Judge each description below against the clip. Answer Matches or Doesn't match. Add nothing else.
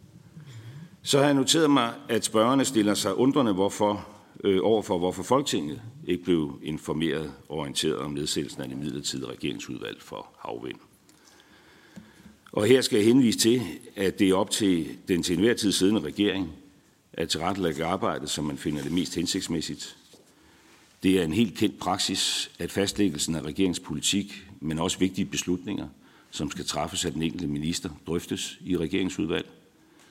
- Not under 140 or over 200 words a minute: Matches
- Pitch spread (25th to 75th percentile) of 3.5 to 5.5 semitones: Matches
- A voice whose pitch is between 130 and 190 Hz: Doesn't match